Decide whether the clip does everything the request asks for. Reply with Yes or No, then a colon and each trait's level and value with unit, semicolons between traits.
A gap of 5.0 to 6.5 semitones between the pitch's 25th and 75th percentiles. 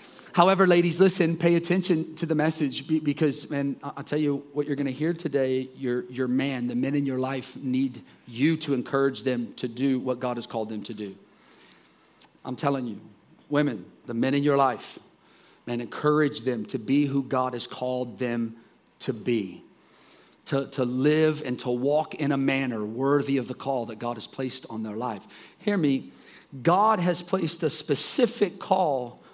No: average, 3.3 semitones